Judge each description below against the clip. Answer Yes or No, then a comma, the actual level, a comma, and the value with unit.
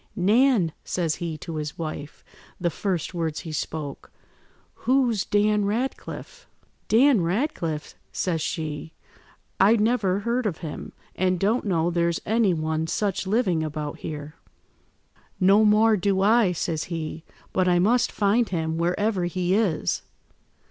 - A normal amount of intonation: Yes, average, 4.7 semitones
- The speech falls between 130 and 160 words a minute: Yes, slow, 135 wpm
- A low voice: No, medium, 185 Hz